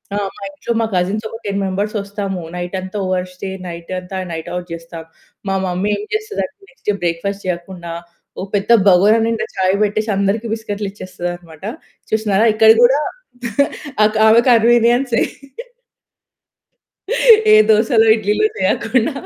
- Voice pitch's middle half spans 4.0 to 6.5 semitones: No, average, 3.4 semitones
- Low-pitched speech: No, high, 200 Hz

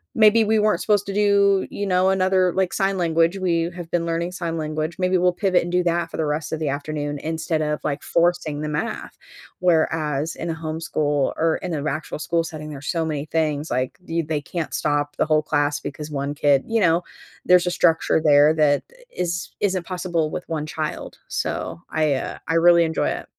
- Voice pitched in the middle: Yes, medium, 165 Hz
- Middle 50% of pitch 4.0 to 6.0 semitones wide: No, average, 2.9 semitones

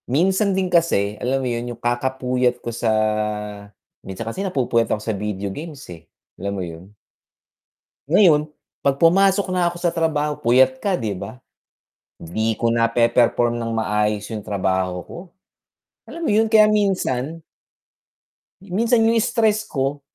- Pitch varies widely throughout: Yes, wide, 8.1 semitones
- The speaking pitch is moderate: No, low, 130 Hz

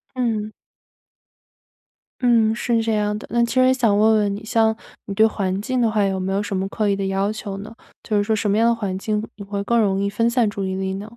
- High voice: Yes, high, 210 Hz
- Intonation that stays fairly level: Yes, narrow, 2.2 semitones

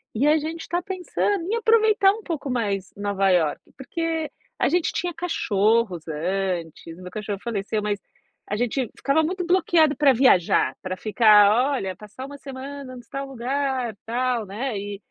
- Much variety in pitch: Yes, wide, 7.4 semitones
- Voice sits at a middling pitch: No, very high, 250 Hz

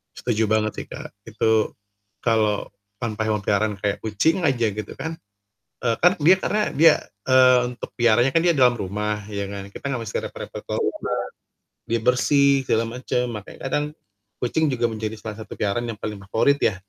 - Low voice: Yes, low, 115 Hz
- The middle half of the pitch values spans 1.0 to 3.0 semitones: No, average, 3.6 semitones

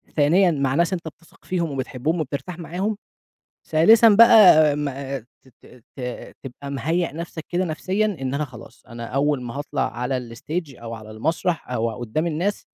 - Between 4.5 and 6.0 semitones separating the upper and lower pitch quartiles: Yes, average, 5.0 semitones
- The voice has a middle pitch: Yes, medium, 150 Hz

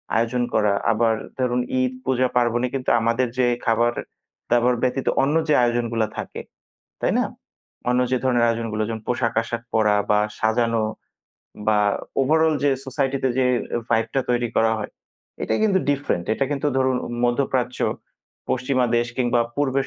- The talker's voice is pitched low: Yes, low, 120 Hz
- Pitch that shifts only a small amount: Yes, narrow, 2.3 semitones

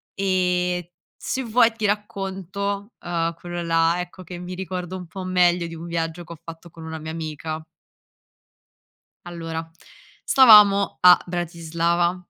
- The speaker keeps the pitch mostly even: Yes, narrow, 2.2 semitones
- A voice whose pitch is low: No, medium, 175 Hz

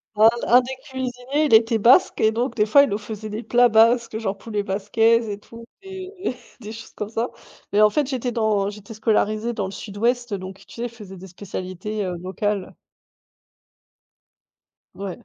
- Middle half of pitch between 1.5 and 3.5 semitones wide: Yes, average, 2.9 semitones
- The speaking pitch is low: No, high, 220 Hz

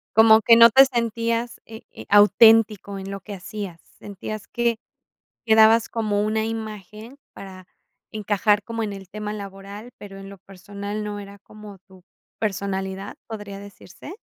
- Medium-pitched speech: No, high, 210 Hz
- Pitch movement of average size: No, narrow, 2.0 semitones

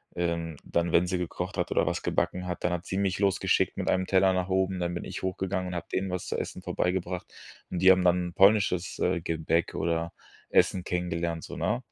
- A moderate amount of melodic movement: No, narrow, 1.6 semitones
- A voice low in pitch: Yes, very low, 90 Hz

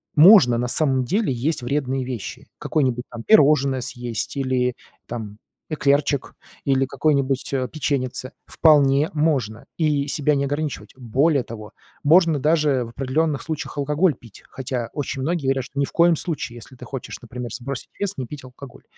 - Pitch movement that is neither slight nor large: Yes, average, 3.1 semitones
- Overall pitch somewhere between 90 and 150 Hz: Yes, low, 135 Hz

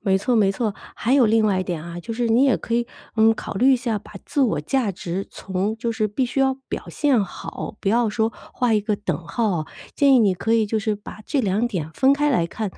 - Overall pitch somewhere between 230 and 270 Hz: No, high, 220 Hz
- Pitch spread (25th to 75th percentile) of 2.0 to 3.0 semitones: No, average, 3.8 semitones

